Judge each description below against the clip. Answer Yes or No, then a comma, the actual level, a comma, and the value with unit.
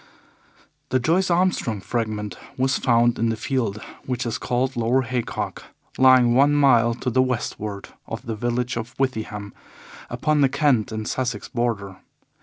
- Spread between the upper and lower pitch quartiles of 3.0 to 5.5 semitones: No, narrow, 2.6 semitones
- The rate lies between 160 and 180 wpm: No, average, 150 wpm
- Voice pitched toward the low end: Yes, low, 120 Hz